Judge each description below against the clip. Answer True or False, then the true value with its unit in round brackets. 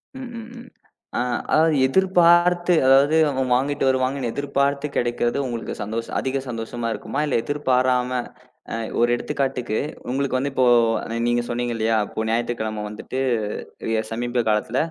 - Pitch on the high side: False (130 Hz)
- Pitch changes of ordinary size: True (3.0 semitones)